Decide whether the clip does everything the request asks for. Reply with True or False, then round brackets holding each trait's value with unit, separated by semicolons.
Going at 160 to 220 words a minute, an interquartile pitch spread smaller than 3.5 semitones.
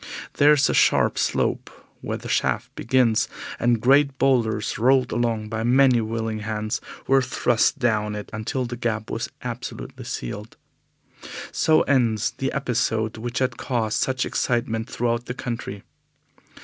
False (145 wpm; 2.8 semitones)